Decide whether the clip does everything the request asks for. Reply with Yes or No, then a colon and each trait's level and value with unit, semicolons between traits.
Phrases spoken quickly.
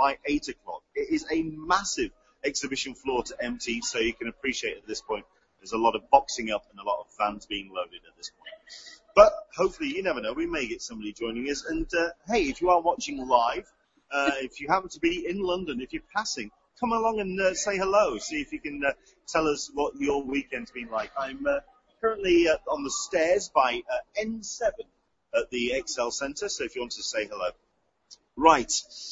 Yes: fast, 215 wpm